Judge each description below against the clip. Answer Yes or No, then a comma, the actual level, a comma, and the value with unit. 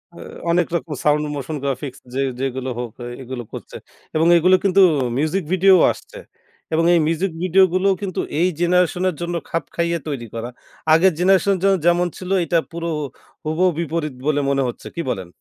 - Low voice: No, medium, 170 Hz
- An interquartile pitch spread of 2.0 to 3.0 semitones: No, average, 4.2 semitones